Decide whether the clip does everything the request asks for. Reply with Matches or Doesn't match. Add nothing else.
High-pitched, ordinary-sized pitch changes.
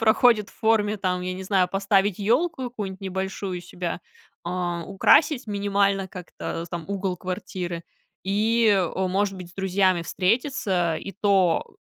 Doesn't match